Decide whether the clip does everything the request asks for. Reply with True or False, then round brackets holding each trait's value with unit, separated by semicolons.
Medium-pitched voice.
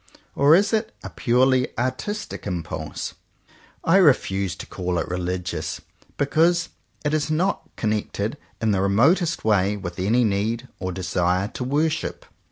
False (110 Hz)